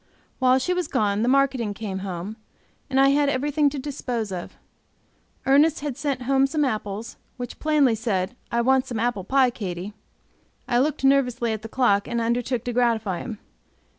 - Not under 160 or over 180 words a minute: Yes, average, 175 wpm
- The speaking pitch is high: Yes, high, 245 Hz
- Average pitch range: Yes, average, 3.9 semitones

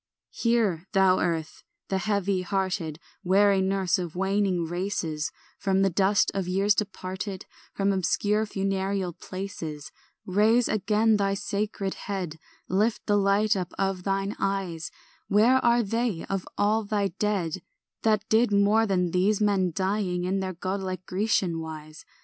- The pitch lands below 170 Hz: No, high, 195 Hz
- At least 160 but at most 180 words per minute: No, average, 145 wpm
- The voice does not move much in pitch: Yes, narrow, 2.0 semitones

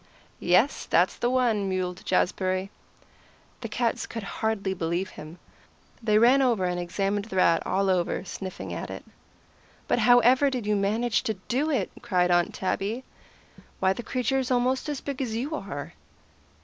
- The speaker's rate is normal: Yes, average, 160 wpm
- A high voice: Yes, high, 215 Hz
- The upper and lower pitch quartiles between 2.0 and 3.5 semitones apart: No, average, 4.7 semitones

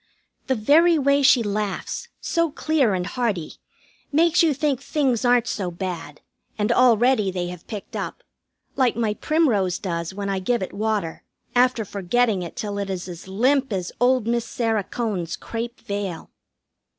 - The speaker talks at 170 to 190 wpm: No, average, 160 wpm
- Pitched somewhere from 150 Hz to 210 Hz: No, high, 220 Hz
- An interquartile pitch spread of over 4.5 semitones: Yes, average, 5.1 semitones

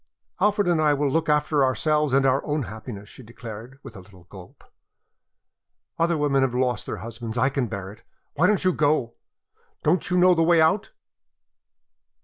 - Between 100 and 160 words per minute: No, average, 180 wpm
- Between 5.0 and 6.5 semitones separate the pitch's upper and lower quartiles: Yes, wide, 5.4 semitones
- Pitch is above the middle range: No, low, 135 Hz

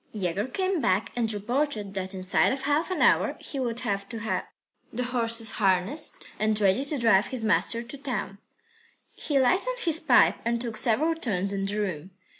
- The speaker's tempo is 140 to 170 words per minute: No, average, 185 wpm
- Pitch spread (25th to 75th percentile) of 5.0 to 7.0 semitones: Yes, average, 5.3 semitones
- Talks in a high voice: Yes, high, 230 Hz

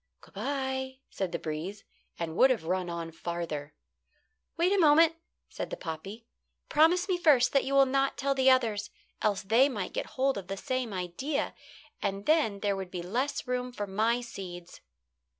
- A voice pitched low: No, high, 230 Hz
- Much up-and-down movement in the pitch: Yes, wide, 6.7 semitones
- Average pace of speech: Yes, average, 180 wpm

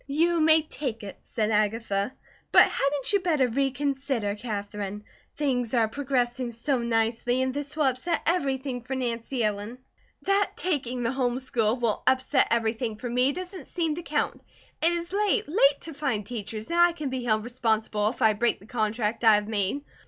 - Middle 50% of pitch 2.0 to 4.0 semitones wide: No, average, 4.4 semitones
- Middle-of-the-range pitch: No, very high, 250 Hz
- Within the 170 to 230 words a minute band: Yes, average, 180 wpm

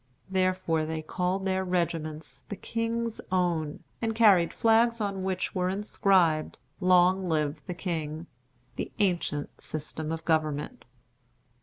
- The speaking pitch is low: No, medium, 180 Hz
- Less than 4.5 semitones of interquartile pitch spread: Yes, average, 3.4 semitones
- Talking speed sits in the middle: No, slow, 125 wpm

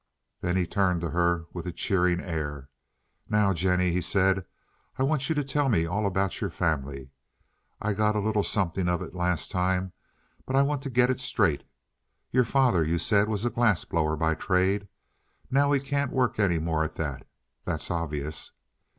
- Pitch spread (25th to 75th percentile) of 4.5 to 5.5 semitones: Yes, average, 4.8 semitones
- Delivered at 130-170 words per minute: No, average, 185 wpm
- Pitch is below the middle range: Yes, very low, 95 Hz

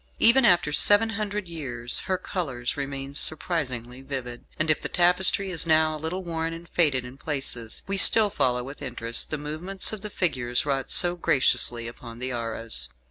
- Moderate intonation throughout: No, wide, 6.2 semitones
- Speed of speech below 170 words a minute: No, average, 180 wpm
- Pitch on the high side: No, medium, 150 Hz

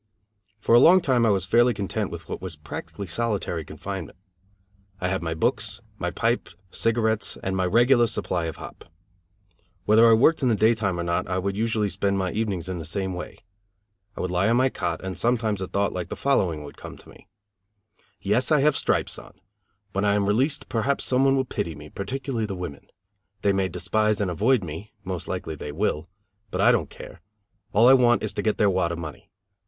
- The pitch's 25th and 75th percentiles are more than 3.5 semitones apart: Yes, average, 4.4 semitones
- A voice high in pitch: No, low, 100 Hz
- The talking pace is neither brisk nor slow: No, fast, 210 wpm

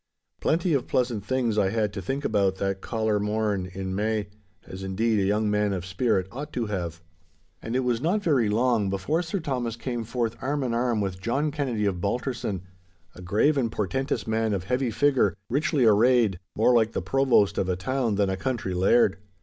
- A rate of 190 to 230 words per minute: Yes, average, 200 wpm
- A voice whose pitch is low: Yes, low, 110 Hz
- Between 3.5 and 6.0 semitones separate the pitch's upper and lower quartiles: Yes, average, 4.4 semitones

